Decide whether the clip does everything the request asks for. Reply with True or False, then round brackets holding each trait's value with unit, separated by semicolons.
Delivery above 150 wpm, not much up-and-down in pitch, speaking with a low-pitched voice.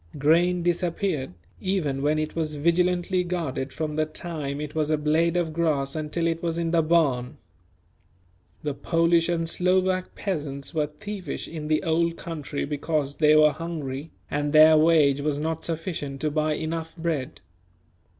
False (160 wpm; 2.2 semitones; 160 Hz)